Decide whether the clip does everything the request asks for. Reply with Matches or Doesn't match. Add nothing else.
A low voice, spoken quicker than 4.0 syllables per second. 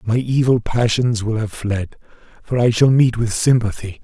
Matches